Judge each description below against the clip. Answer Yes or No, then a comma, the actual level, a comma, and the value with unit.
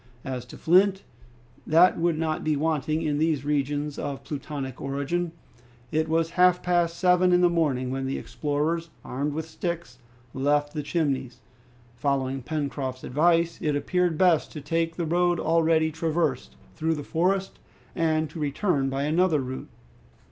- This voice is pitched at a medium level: Yes, medium, 155 Hz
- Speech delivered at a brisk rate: No, average, 155 wpm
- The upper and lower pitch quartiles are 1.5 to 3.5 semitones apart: Yes, average, 3.1 semitones